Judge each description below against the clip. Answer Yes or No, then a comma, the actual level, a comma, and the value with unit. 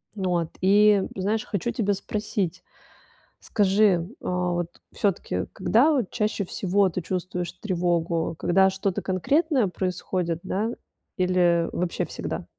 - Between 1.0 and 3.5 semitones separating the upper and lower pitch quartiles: Yes, average, 2.8 semitones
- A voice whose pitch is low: No, medium, 185 Hz